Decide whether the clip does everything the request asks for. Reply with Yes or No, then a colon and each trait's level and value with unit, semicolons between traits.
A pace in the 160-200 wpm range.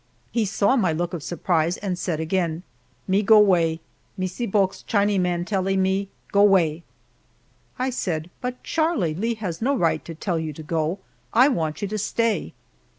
Yes: average, 175 wpm